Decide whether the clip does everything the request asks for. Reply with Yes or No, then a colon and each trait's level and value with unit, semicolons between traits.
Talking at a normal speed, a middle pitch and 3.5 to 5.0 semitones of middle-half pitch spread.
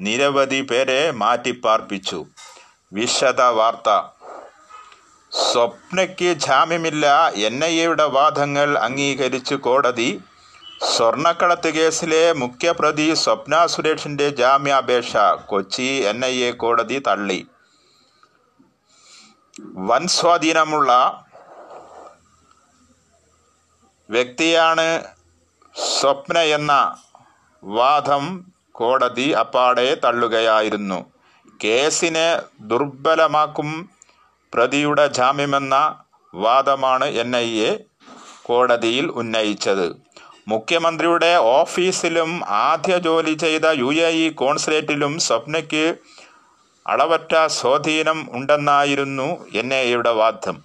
Yes: average, 70 wpm; medium, 145 Hz; average, 4.5 semitones